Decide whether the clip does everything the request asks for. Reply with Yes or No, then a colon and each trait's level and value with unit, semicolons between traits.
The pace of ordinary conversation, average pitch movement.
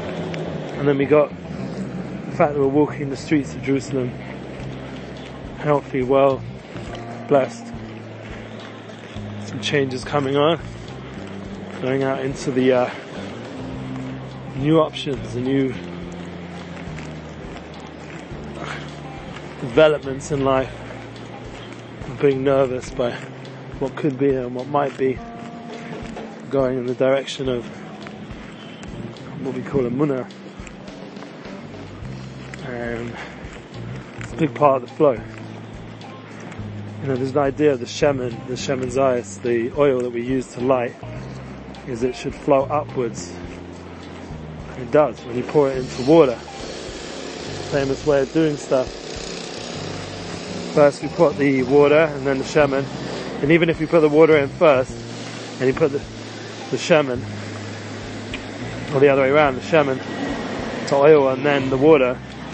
No: slow, 130 wpm; average, 3.9 semitones